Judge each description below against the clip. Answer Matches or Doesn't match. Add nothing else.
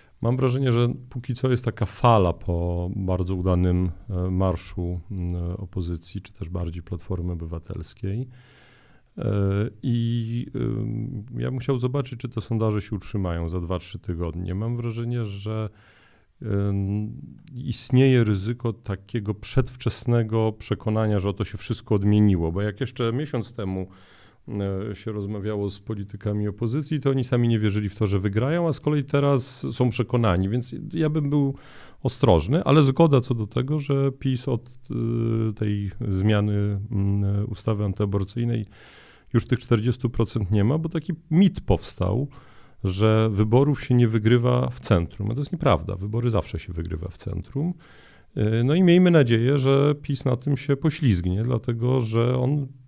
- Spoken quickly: Doesn't match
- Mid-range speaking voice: Doesn't match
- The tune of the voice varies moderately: Matches